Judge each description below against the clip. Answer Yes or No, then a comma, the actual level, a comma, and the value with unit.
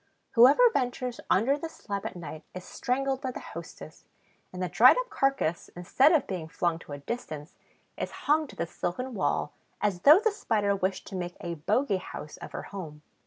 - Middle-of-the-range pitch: No, high, 205 Hz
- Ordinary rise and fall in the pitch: No, wide, 7.5 semitones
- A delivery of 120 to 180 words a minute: No, average, 195 wpm